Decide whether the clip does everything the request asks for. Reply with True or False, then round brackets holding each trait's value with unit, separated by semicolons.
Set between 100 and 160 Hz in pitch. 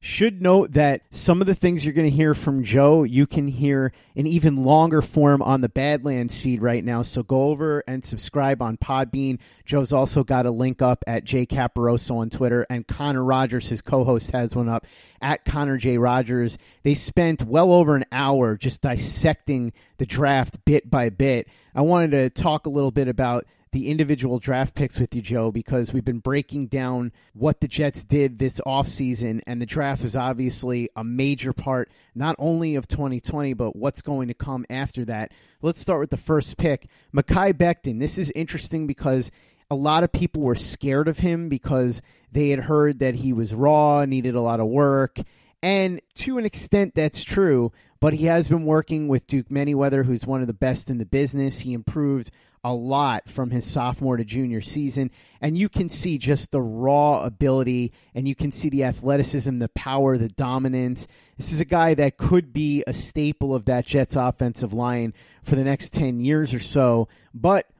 True (135 Hz)